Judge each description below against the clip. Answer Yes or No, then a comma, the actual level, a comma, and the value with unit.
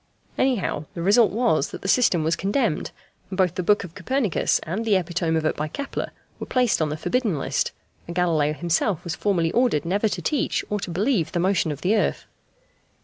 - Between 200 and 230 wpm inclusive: Yes, fast, 205 wpm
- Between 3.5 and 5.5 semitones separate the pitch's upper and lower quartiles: Yes, average, 4.7 semitones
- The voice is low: No, medium, 185 Hz